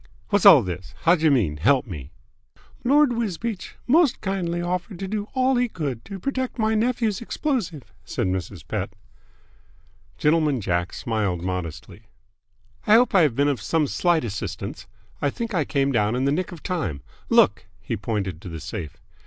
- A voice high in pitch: No, medium, 150 Hz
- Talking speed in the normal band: Yes, average, 165 wpm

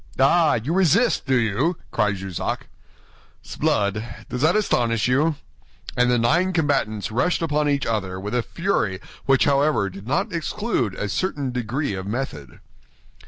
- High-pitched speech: No, low, 130 Hz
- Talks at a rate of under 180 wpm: Yes, average, 150 wpm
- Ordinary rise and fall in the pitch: No, wide, 6.8 semitones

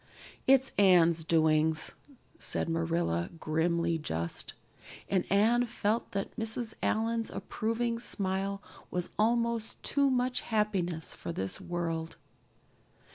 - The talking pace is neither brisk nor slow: No, slow, 105 wpm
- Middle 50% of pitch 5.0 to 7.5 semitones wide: Yes, wide, 5.6 semitones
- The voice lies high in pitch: Yes, high, 195 Hz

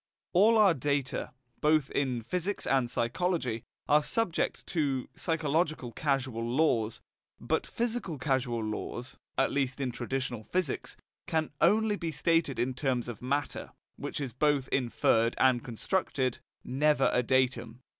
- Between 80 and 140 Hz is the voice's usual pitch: Yes, low, 135 Hz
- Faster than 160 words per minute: No, slow, 135 wpm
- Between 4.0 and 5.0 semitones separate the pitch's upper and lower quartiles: Yes, average, 4.4 semitones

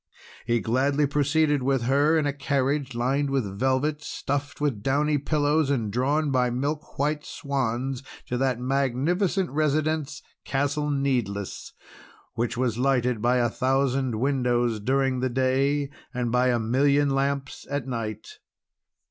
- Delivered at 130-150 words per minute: Yes, average, 140 wpm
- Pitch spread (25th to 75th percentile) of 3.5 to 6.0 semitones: No, narrow, 2.5 semitones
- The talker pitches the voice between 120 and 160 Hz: Yes, low, 135 Hz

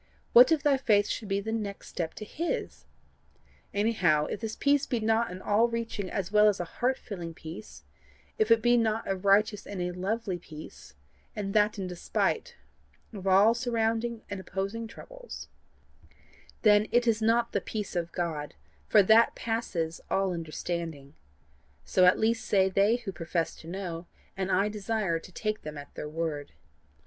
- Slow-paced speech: No, average, 175 wpm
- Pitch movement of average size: Yes, average, 4.2 semitones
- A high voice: Yes, high, 205 Hz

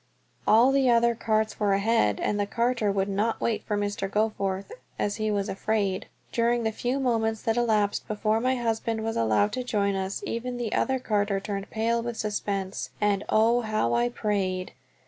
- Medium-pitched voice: No, high, 215 Hz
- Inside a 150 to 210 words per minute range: Yes, average, 180 wpm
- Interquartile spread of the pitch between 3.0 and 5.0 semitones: No, narrow, 2.6 semitones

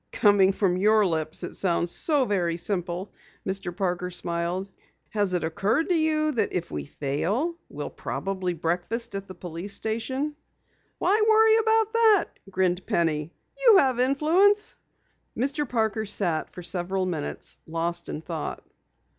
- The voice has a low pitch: No, high, 195 Hz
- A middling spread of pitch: No, wide, 7.7 semitones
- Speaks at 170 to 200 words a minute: No, average, 145 wpm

